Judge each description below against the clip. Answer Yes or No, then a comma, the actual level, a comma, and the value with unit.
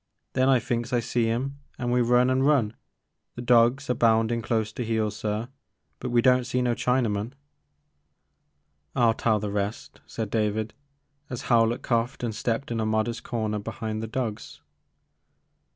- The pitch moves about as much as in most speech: No, narrow, 2.1 semitones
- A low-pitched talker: Yes, low, 115 Hz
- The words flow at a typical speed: Yes, average, 170 wpm